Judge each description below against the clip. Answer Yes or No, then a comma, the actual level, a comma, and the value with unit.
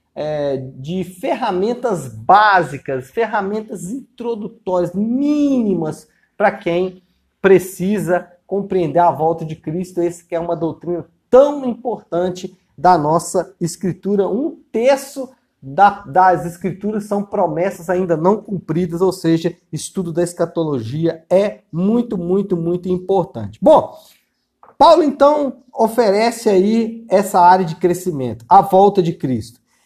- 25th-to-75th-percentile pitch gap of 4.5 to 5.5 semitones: No, average, 3.7 semitones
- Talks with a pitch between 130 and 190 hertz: Yes, medium, 185 Hz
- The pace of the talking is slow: Yes, slow, 115 wpm